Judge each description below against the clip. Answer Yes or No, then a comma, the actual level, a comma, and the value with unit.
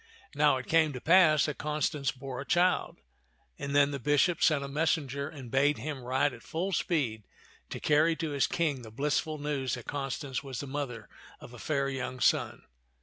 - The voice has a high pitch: No, medium, 145 Hz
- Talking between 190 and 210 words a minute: Yes, average, 195 wpm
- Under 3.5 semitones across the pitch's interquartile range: Yes, narrow, 2.4 semitones